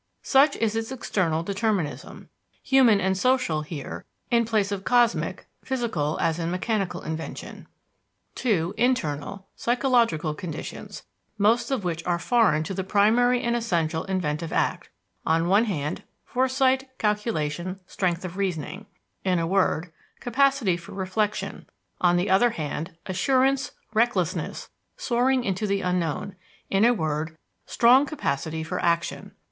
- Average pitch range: No, wide, 6.0 semitones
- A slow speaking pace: Yes, slow, 130 wpm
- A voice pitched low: No, high, 195 Hz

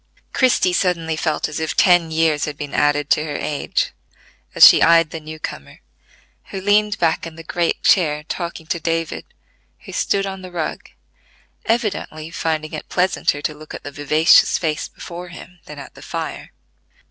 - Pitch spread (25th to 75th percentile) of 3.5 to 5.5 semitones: No, narrow, 2.6 semitones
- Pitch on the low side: No, medium, 160 Hz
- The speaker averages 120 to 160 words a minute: No, average, 175 wpm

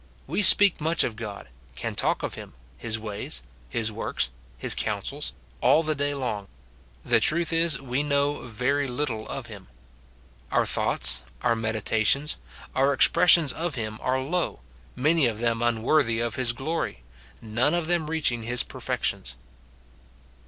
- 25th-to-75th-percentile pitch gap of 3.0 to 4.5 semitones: No, average, 5.3 semitones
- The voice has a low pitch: Yes, low, 130 Hz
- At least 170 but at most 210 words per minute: No, average, 150 wpm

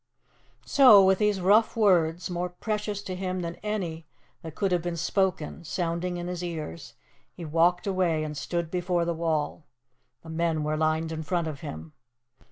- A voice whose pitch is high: No, medium, 175 Hz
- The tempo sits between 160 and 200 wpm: Yes, average, 175 wpm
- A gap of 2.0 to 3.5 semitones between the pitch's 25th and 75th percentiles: Yes, narrow, 2.6 semitones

